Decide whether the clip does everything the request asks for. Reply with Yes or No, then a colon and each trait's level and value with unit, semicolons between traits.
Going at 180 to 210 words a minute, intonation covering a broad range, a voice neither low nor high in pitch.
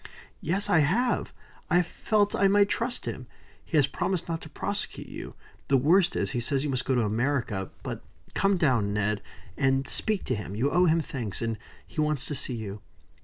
Yes: average, 200 wpm; wide, 7.1 semitones; medium, 145 Hz